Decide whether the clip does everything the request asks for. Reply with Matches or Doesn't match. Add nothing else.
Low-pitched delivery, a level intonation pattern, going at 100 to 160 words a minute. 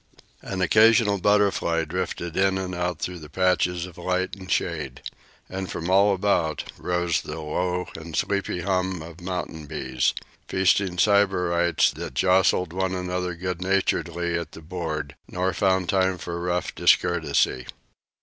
Matches